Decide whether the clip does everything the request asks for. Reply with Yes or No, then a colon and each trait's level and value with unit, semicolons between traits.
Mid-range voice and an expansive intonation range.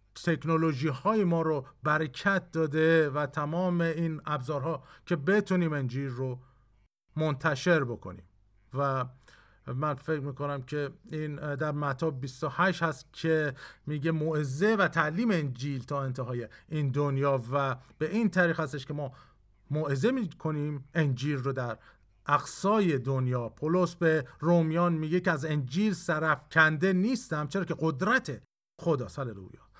No: medium, 150 Hz; average, 3.2 semitones